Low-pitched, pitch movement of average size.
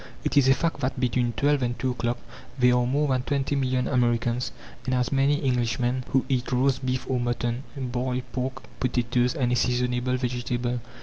No: low, 125 Hz; narrow, 1.4 semitones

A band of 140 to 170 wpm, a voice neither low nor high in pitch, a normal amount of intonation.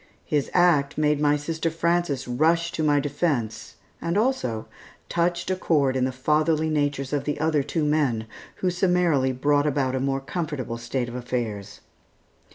Yes: average, 165 wpm; medium, 145 Hz; average, 3.9 semitones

